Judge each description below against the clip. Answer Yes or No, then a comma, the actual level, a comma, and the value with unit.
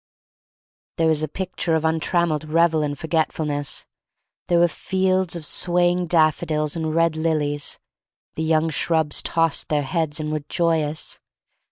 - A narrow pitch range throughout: Yes, narrow, 1.8 semitones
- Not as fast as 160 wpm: Yes, average, 140 wpm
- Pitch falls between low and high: Yes, medium, 160 Hz